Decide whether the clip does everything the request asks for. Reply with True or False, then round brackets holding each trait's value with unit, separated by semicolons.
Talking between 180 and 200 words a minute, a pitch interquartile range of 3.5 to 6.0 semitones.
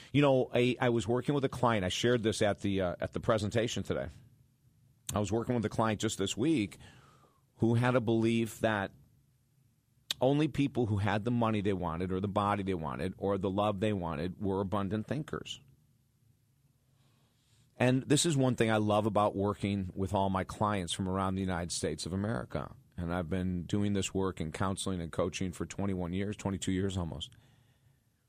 True (190 wpm; 4.5 semitones)